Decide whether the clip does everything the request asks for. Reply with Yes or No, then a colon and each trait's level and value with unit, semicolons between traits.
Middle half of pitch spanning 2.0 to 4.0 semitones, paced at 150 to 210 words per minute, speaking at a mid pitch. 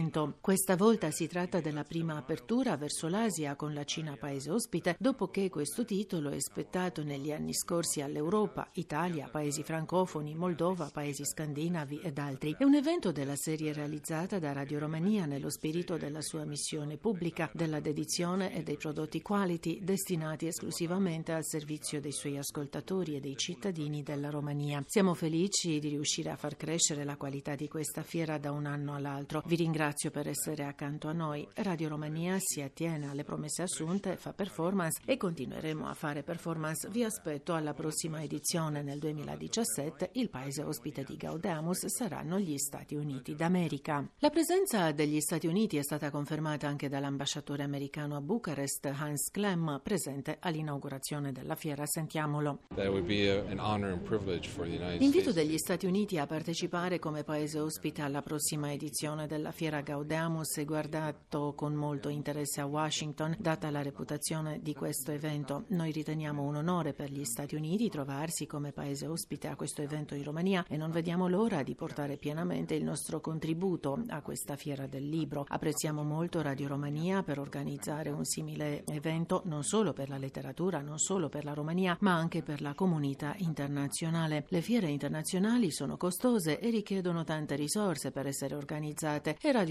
Yes: average, 2.9 semitones; average, 160 wpm; medium, 155 Hz